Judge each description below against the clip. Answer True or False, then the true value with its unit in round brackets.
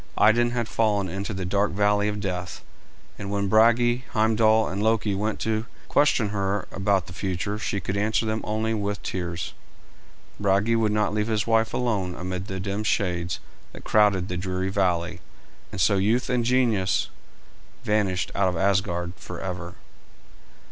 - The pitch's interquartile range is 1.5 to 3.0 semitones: True (2.7 semitones)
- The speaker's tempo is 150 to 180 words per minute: True (160 wpm)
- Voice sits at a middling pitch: False (100 Hz)